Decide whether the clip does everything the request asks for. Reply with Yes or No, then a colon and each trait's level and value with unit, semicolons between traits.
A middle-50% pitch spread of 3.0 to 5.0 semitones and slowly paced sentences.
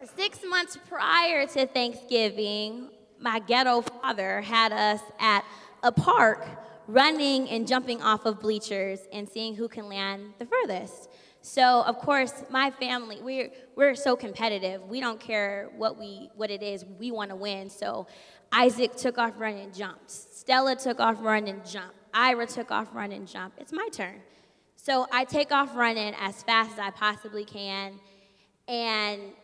No: average, 3.5 semitones; average, 165 wpm